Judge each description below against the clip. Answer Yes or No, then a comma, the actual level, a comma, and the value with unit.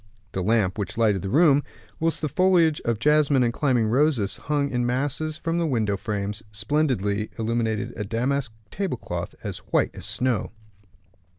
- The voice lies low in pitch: Yes, low, 125 Hz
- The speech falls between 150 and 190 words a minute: Yes, average, 165 wpm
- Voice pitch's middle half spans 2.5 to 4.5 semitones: No, wide, 5.6 semitones